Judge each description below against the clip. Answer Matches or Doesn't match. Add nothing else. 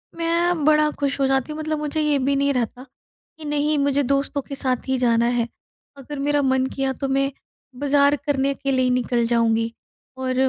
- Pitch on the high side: Matches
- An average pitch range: Doesn't match